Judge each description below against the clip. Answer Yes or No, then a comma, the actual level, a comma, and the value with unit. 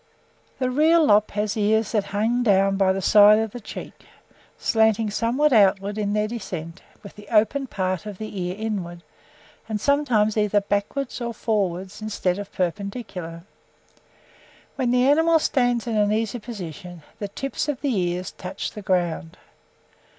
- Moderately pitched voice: No, high, 210 Hz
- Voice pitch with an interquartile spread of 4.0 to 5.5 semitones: No, average, 3.5 semitones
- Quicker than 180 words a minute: No, average, 160 wpm